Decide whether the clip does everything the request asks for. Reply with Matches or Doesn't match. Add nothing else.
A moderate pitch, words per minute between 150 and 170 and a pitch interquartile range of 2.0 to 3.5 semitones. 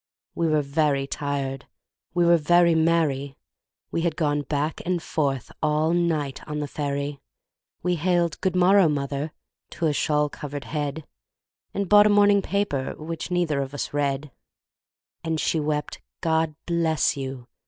Matches